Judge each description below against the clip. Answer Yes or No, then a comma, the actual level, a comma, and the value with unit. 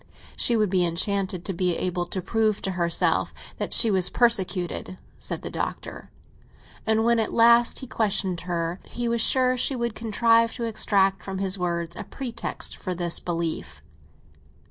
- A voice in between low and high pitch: No, high, 195 Hz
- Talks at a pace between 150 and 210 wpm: Yes, average, 165 wpm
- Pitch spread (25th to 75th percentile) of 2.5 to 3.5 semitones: No, average, 4.3 semitones